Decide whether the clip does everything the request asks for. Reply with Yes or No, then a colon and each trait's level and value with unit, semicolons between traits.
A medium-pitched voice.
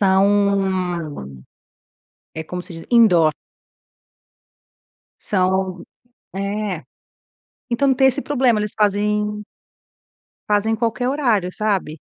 No: high, 205 Hz